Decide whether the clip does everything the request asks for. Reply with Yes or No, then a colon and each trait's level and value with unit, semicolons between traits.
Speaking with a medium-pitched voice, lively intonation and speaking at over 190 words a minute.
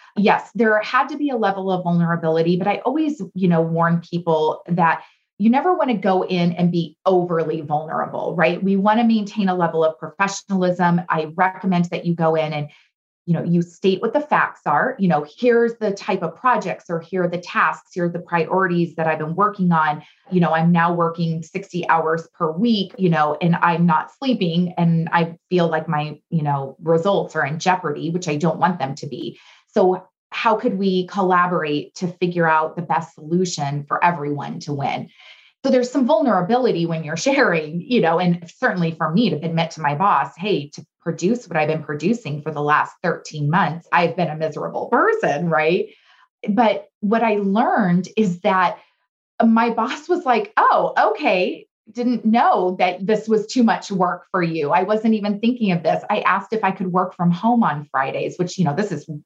No: medium, 175 Hz; average, 4.1 semitones; average, 200 wpm